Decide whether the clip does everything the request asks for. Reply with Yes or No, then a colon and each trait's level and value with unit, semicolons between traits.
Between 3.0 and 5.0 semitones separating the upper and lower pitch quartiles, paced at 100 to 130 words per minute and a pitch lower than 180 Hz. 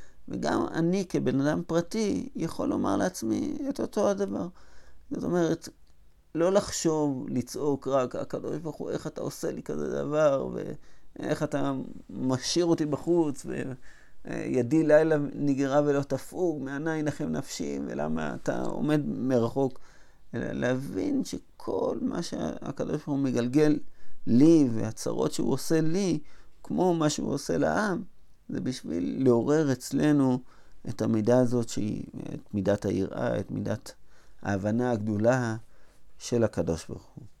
No: wide, 5.4 semitones; average, 125 wpm; low, 135 Hz